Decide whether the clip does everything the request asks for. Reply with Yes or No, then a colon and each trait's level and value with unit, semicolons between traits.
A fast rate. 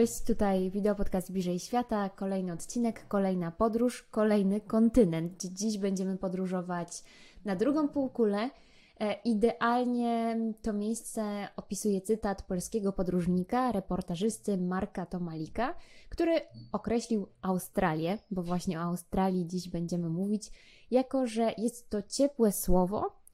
No: average, 115 wpm